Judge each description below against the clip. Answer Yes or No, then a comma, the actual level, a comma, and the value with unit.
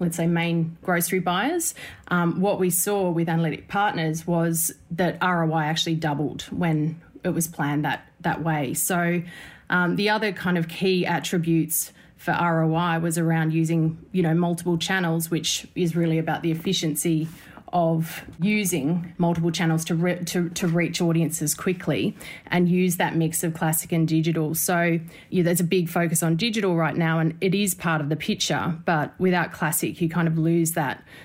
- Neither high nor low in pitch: Yes, medium, 170 Hz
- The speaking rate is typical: Yes, average, 175 wpm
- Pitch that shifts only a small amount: Yes, narrow, 1.6 semitones